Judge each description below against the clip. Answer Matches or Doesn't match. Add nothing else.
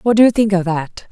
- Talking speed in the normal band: Doesn't match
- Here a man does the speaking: Doesn't match